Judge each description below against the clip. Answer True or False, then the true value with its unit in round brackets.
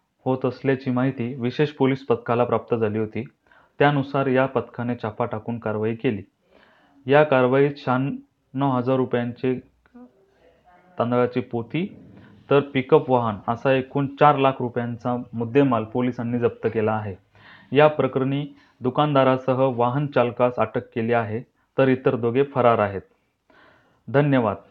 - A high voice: False (125 Hz)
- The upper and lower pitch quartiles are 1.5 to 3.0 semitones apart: True (2.7 semitones)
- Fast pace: False (120 wpm)